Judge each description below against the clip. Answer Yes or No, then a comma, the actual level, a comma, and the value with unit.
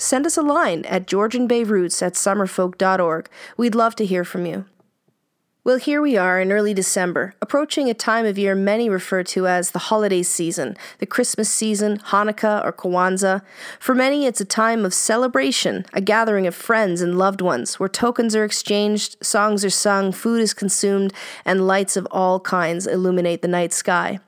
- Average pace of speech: Yes, average, 180 wpm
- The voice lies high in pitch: Yes, high, 200 Hz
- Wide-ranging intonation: No, average, 3.1 semitones